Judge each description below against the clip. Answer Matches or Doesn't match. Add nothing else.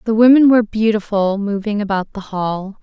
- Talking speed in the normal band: Matches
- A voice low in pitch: Doesn't match